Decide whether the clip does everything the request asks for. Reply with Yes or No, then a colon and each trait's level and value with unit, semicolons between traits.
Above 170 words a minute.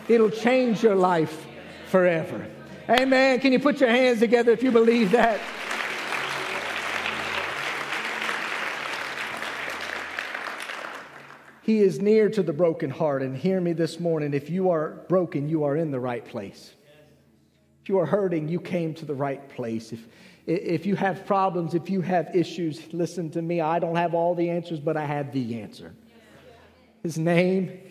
No: average, 155 wpm